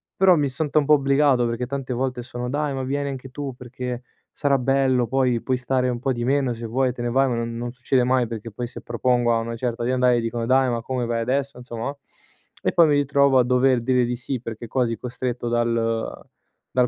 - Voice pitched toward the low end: Yes, low, 125 Hz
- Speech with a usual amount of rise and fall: No, narrow, 2.1 semitones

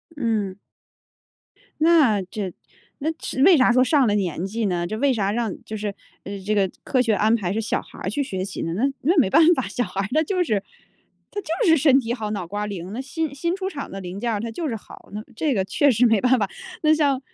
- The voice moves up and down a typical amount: No, wide, 5.8 semitones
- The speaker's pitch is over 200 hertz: Yes, high, 225 Hz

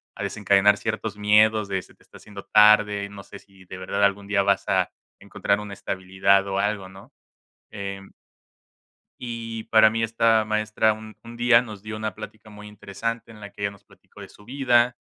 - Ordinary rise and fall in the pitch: No, narrow, 1.9 semitones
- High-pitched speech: No, low, 105 Hz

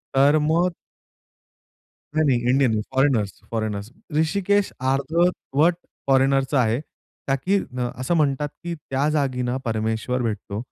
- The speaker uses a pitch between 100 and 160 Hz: Yes, low, 135 Hz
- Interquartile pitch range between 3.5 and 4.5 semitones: Yes, average, 4.1 semitones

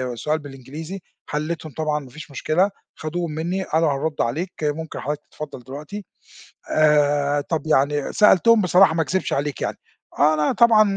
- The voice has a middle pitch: Yes, medium, 155 Hz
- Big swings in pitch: No, narrow, 2.6 semitones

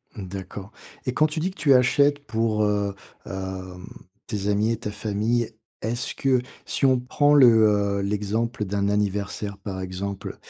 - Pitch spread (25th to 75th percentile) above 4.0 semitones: No, average, 3.4 semitones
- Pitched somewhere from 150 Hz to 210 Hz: No, low, 105 Hz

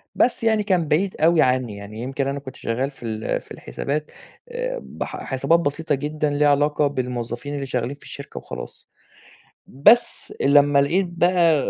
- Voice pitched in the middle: Yes, medium, 145 Hz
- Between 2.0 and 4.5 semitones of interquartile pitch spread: Yes, average, 4.2 semitones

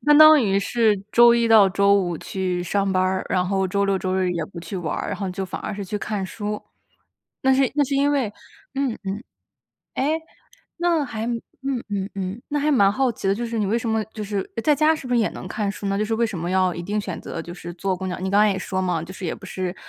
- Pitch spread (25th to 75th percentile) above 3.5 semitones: Yes, average, 4.0 semitones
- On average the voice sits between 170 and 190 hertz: No, high, 200 Hz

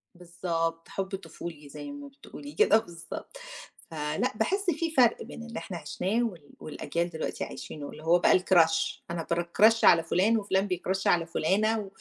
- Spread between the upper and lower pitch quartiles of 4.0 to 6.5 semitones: Yes, average, 5.1 semitones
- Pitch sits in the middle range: Yes, medium, 180 Hz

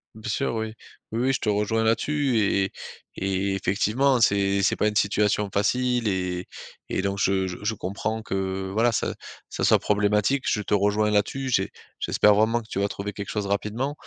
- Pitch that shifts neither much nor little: No, narrow, 2.2 semitones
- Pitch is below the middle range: Yes, low, 105 Hz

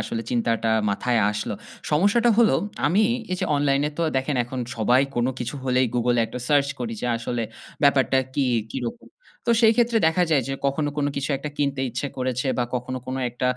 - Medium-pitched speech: No, low, 130 Hz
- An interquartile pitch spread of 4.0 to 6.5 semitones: No, average, 3.2 semitones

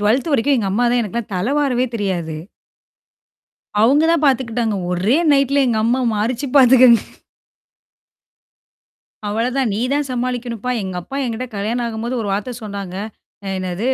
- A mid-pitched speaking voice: No, high, 235 Hz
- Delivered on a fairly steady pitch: No, average, 3.7 semitones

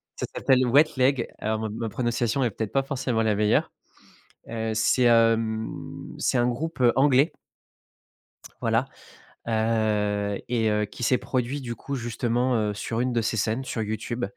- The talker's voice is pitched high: No, low, 115 Hz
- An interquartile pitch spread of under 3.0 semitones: Yes, narrow, 2.5 semitones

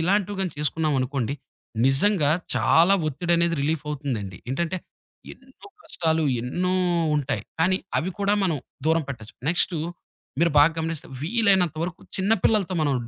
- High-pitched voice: No, medium, 165 Hz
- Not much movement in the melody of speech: No, average, 4.4 semitones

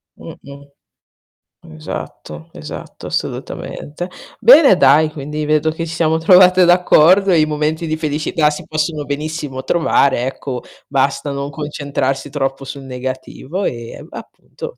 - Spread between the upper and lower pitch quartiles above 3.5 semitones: No, average, 2.8 semitones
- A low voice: No, medium, 150 Hz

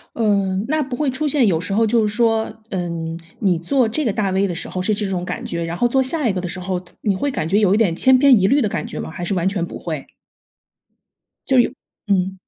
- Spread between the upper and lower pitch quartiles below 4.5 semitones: No, average, 5.0 semitones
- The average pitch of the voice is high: Yes, high, 200 Hz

